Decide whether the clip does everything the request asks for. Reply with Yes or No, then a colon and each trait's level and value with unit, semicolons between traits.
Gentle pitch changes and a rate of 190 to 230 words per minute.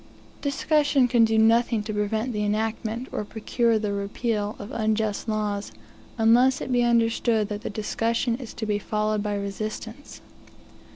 No: narrow, 2.0 semitones; average, 155 wpm